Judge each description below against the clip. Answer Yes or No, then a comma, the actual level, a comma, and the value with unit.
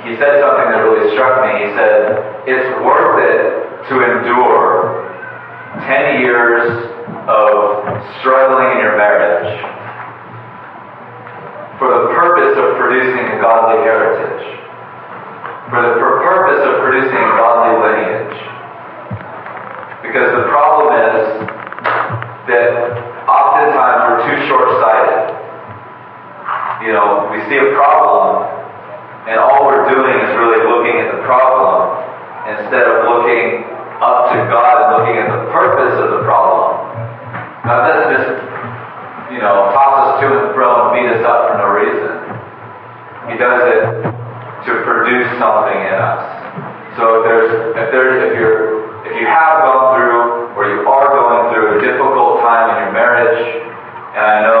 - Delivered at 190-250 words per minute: No, average, 140 wpm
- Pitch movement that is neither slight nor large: No, wide, 5.7 semitones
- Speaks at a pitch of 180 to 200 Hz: No, low, 120 Hz